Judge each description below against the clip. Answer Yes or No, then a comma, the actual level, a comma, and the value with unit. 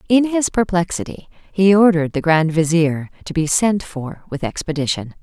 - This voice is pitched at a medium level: Yes, medium, 175 Hz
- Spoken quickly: No, average, 160 wpm